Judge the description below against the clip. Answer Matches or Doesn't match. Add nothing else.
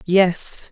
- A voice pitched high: Doesn't match